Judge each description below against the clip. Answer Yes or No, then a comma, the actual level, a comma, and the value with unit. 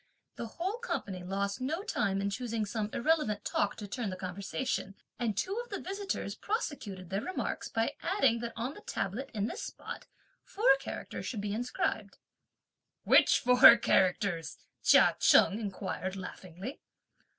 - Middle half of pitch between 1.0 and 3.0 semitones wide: No, wide, 5.5 semitones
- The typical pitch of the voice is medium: No, high, 225 Hz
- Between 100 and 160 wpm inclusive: Yes, average, 150 wpm